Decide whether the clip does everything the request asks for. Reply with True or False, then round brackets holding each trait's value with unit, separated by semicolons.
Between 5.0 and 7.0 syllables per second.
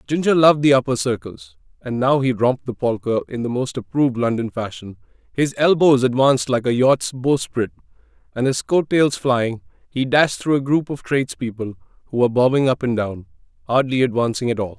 True (5.6 syllables/s)